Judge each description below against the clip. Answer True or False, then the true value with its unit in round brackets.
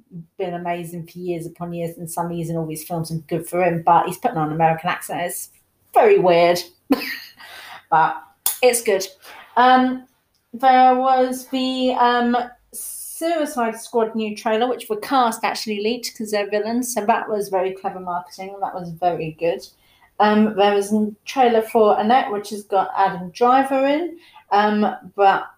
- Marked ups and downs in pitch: True (5.8 semitones)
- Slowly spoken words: False (165 wpm)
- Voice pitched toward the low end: False (205 Hz)